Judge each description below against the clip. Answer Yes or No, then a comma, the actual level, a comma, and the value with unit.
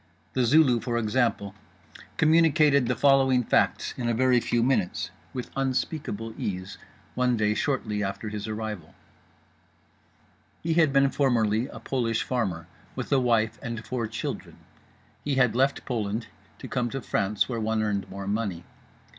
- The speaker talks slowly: No, average, 150 wpm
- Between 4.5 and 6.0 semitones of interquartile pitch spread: No, average, 3.7 semitones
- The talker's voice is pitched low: Yes, low, 120 Hz